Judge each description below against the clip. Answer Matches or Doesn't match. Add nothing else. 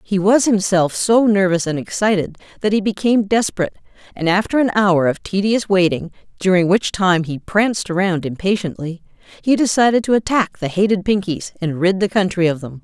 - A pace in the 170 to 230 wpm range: Matches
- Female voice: Matches